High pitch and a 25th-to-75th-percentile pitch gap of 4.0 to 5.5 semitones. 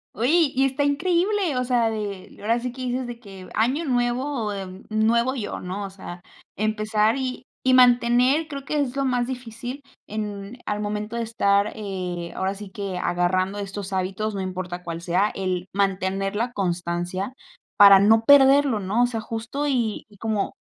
Yes: high, 215 Hz; average, 4.4 semitones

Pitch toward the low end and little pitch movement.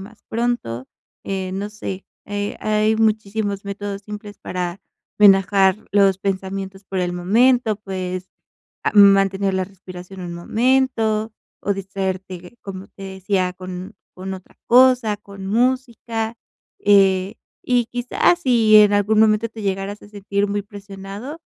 No: high, 200 Hz; narrow, 2.2 semitones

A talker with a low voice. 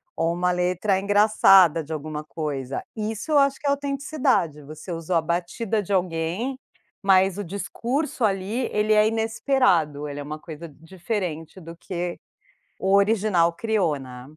No: medium, 185 Hz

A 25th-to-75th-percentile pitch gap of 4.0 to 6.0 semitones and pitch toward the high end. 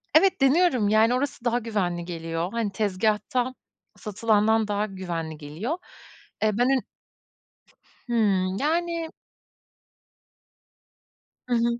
Yes: average, 4.8 semitones; high, 220 Hz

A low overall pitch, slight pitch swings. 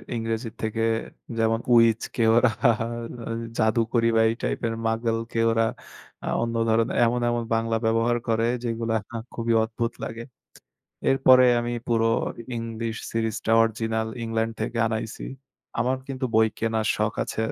Yes: low, 115 Hz; narrow, 0.7 semitones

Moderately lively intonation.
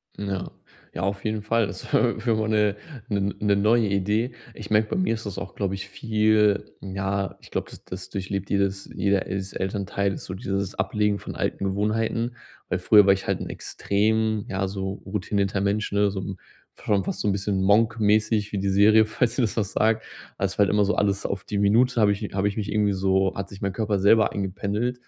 No: narrow, 1.7 semitones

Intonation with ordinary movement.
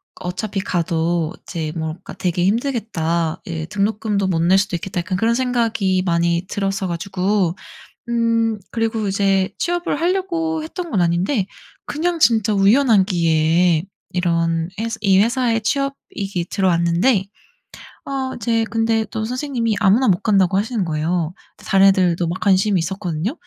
Yes: average, 4.7 semitones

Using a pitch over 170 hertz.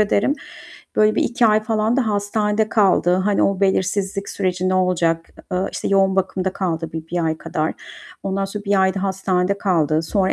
Yes: high, 190 Hz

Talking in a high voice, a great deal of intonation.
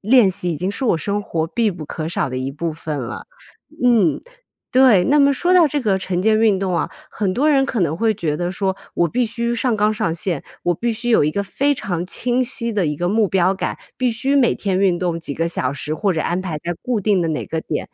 Yes: high, 195 Hz; wide, 5.7 semitones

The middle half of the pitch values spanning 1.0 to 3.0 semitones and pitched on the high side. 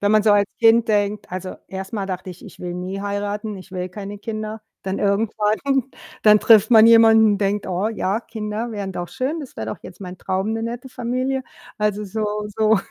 Yes: narrow, 2.5 semitones; high, 210 Hz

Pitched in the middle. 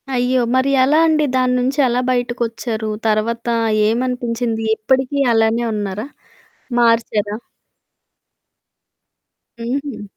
No: high, 240 Hz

